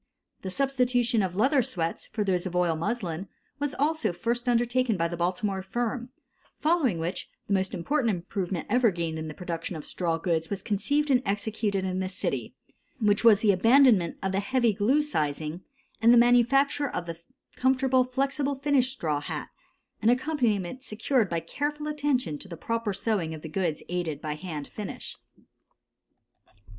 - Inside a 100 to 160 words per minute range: No, average, 170 wpm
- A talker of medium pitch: No, high, 210 Hz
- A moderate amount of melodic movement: No, wide, 6.5 semitones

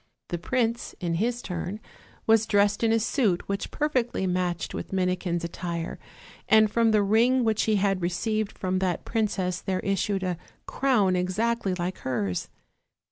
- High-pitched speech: Yes, high, 195 Hz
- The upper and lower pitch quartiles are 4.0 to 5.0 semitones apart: No, average, 3.6 semitones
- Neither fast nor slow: Yes, average, 160 wpm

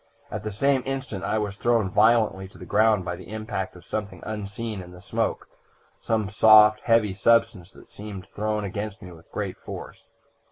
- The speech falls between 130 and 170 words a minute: No, average, 185 wpm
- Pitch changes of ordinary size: No, narrow, 2.2 semitones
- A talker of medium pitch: No, low, 105 Hz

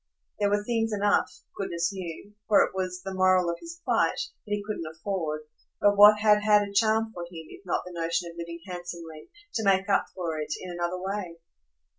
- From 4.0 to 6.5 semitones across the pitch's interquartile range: No, average, 3.3 semitones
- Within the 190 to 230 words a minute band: Yes, fast, 205 wpm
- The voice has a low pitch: No, medium, 185 Hz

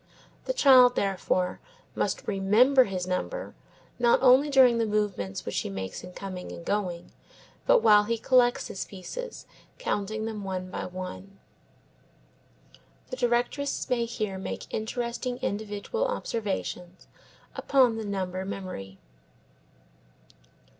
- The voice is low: No, high, 210 Hz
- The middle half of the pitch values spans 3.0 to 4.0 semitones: No, average, 4.9 semitones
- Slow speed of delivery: Yes, slow, 120 wpm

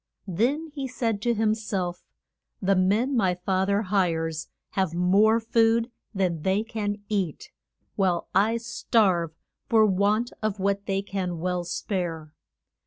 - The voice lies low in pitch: No, high, 200 Hz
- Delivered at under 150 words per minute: Yes, average, 140 wpm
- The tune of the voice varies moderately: Yes, average, 3.5 semitones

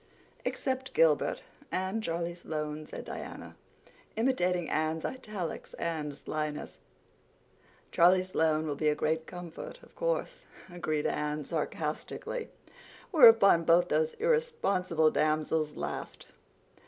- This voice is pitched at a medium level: Yes, medium, 170 Hz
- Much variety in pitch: Yes, wide, 6.3 semitones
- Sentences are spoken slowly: Yes, slow, 105 wpm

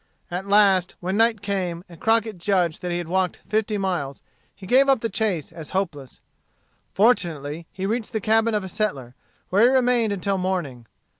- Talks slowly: No, average, 180 wpm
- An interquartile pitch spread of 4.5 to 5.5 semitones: No, average, 4.0 semitones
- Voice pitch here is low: No, high, 195 Hz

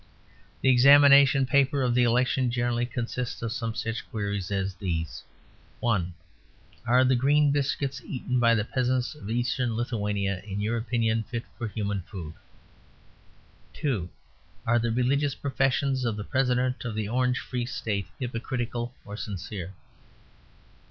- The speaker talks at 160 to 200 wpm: No, average, 140 wpm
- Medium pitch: No, low, 120 Hz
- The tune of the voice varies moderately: Yes, average, 3.2 semitones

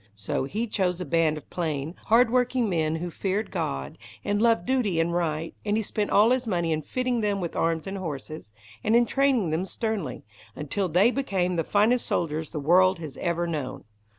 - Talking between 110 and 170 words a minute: No, average, 200 wpm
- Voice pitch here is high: No, medium, 180 Hz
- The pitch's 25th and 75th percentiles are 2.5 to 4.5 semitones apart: No, average, 5.3 semitones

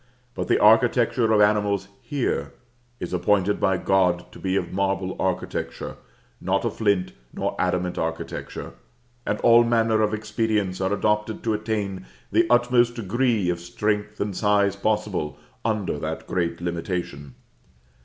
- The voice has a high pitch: No, low, 105 Hz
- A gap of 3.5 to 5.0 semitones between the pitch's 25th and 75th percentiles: No, average, 2.9 semitones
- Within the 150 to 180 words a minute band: No, average, 140 wpm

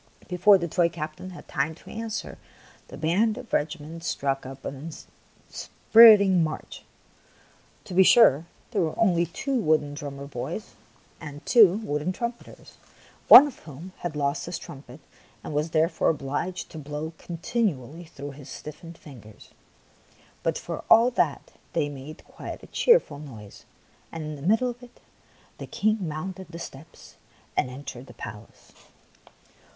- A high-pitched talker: No, medium, 160 Hz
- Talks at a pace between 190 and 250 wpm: No, average, 155 wpm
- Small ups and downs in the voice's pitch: No, average, 4.8 semitones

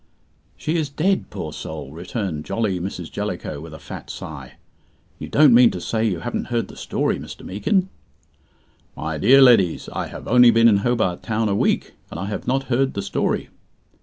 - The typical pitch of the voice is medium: No, low, 110 Hz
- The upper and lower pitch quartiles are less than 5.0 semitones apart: No, wide, 5.4 semitones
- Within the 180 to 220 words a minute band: Yes, average, 190 wpm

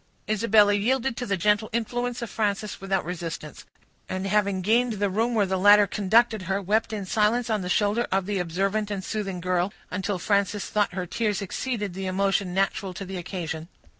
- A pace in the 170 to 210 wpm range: Yes, average, 190 wpm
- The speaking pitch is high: Yes, high, 200 Hz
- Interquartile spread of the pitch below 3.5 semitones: Yes, narrow, 2.5 semitones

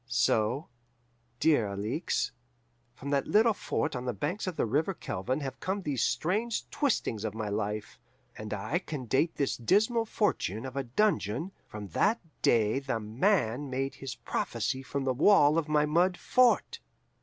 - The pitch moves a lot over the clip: Yes, wide, 7.9 semitones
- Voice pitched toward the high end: No, low, 135 Hz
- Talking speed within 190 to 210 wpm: No, average, 165 wpm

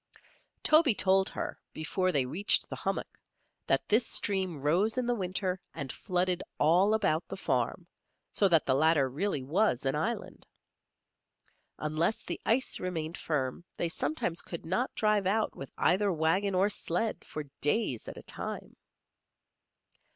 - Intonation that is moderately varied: Yes, average, 4.8 semitones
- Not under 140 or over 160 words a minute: Yes, average, 150 wpm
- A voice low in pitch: No, medium, 180 Hz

